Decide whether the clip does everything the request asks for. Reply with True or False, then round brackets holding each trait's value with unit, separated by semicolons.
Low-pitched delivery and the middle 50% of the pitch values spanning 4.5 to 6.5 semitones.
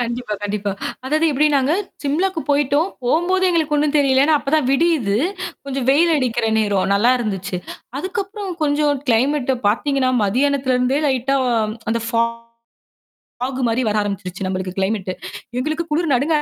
False (270 Hz; 4.9 semitones)